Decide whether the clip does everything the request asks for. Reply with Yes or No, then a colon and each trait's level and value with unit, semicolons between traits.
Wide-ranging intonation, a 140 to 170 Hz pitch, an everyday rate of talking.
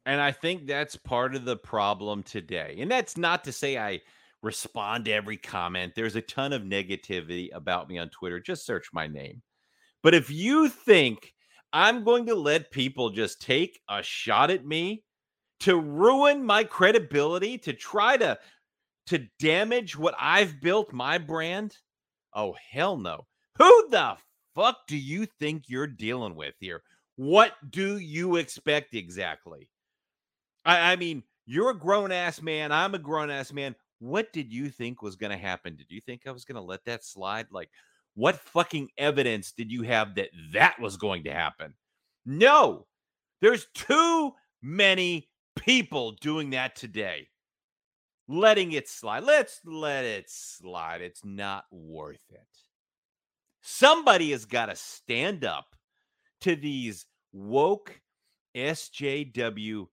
Yes: wide, 8.4 semitones; medium, 145 Hz; average, 150 wpm